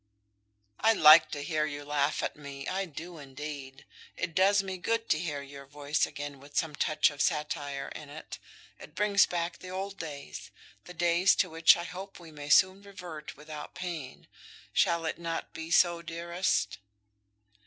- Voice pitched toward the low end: No, medium, 160 Hz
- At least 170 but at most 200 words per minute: Yes, average, 175 wpm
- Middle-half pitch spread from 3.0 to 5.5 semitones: Yes, average, 3.6 semitones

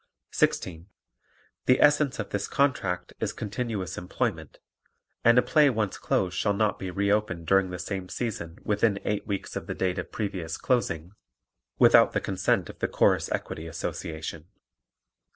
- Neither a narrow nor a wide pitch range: Yes, average, 3.8 semitones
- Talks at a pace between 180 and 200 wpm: No, average, 155 wpm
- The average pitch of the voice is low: Yes, low, 100 Hz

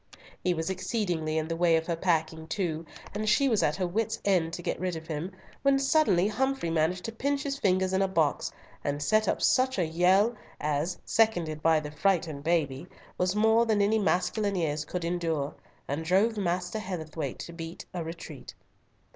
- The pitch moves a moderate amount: Yes, average, 4.4 semitones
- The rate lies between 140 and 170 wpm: No, average, 190 wpm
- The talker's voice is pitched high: No, medium, 180 Hz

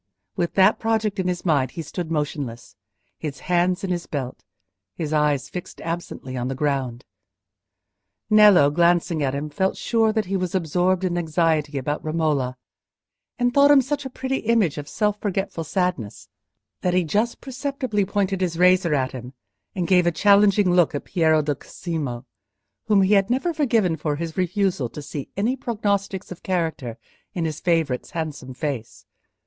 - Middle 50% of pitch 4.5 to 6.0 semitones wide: Yes, average, 5.2 semitones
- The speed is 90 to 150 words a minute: No, average, 165 wpm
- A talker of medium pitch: Yes, medium, 175 Hz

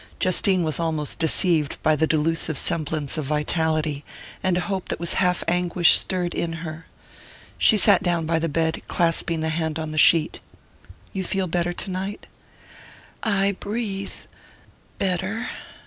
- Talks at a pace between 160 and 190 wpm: No, average, 145 wpm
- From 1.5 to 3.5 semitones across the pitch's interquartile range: Yes, average, 2.8 semitones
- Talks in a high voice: No, medium, 170 Hz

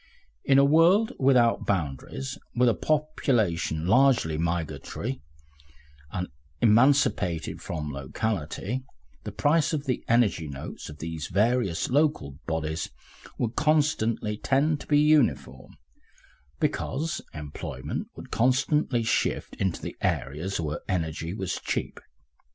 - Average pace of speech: No, slow, 115 wpm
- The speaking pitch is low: Yes, low, 110 Hz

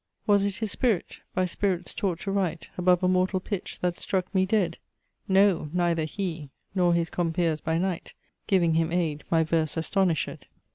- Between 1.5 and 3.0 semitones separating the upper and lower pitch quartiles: Yes, narrow, 2.6 semitones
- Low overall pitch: No, medium, 180 Hz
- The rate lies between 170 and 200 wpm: Yes, average, 175 wpm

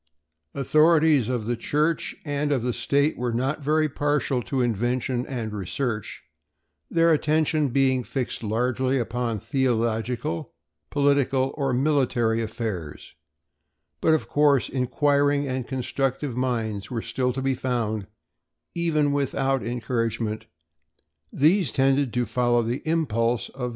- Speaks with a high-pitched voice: No, low, 130 Hz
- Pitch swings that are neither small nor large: Yes, average, 3.3 semitones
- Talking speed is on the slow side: Yes, slow, 130 wpm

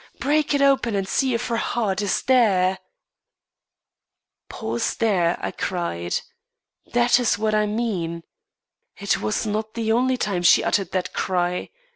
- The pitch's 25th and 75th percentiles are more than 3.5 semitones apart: Yes, average, 4.7 semitones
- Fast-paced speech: No, average, 145 wpm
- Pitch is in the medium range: No, high, 210 Hz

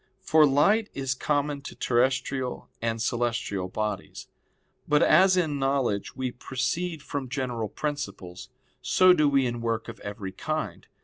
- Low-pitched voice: Yes, low, 130 Hz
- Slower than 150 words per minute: Yes, average, 140 wpm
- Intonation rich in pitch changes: No, average, 4.1 semitones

